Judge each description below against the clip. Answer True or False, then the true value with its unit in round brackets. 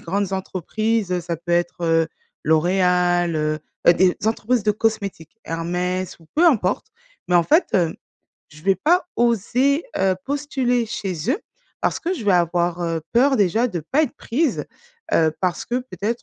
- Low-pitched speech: False (190 Hz)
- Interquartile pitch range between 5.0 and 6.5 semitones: True (5.5 semitones)